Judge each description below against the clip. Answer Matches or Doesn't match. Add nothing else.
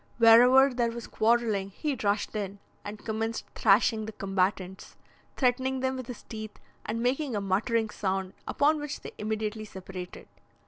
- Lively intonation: Doesn't match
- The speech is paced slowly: Doesn't match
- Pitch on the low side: Doesn't match